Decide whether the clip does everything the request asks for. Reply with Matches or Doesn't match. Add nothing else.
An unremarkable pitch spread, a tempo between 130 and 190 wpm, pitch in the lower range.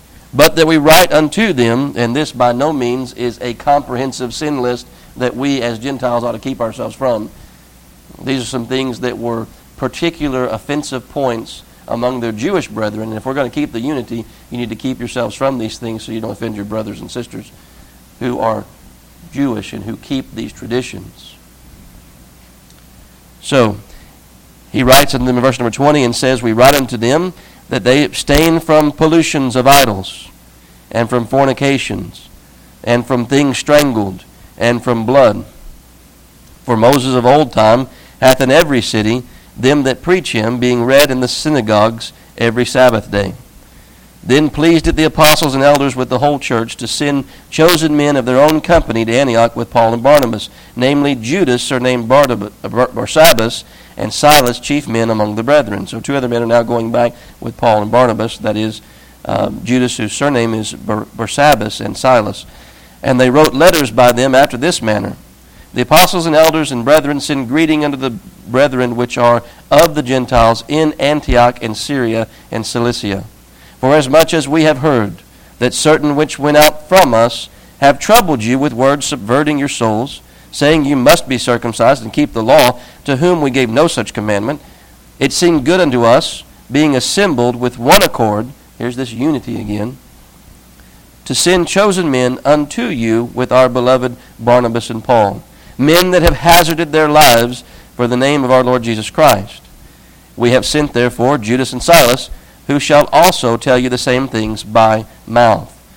Matches